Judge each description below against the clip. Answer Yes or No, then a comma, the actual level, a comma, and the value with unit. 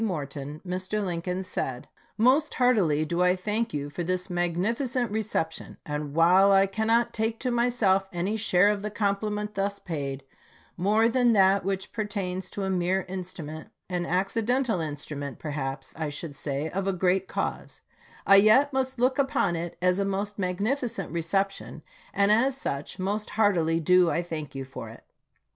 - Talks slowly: No, average, 165 wpm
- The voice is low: No, high, 190 Hz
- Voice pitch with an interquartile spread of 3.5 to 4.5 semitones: Yes, average, 4.2 semitones